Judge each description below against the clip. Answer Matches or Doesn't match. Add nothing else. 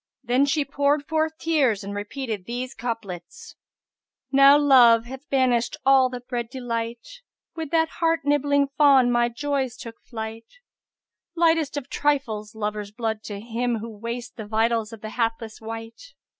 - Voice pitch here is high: Matches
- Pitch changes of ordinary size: Matches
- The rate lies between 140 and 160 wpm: Matches